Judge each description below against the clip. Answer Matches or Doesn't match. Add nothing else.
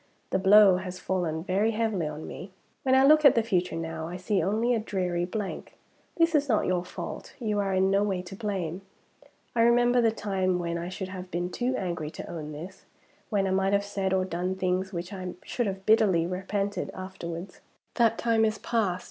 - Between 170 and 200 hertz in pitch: Matches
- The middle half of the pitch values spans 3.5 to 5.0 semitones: Doesn't match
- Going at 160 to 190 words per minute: Doesn't match